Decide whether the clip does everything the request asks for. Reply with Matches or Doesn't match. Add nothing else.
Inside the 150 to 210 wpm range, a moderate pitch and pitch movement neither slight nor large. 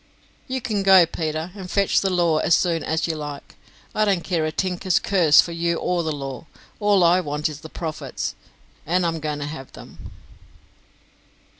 Matches